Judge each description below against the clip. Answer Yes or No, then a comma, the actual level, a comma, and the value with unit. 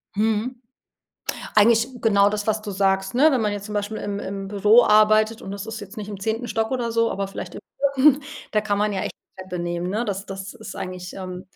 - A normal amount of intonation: No, narrow, 2.3 semitones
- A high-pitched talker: Yes, high, 210 Hz